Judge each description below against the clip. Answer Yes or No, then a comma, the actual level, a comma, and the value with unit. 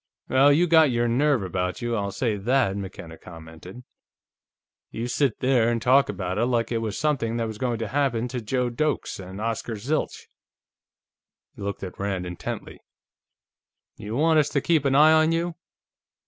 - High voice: No, low, 120 Hz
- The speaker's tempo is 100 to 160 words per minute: No, average, 175 wpm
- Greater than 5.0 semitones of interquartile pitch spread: Yes, wide, 5.5 semitones